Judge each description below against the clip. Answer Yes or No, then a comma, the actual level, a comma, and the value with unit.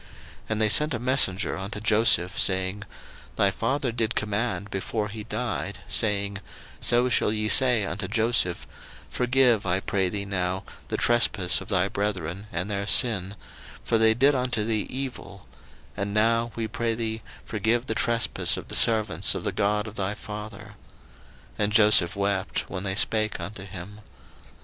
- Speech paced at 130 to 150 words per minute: No, average, 165 wpm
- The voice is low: Yes, low, 105 Hz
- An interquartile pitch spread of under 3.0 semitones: Yes, narrow, 2.6 semitones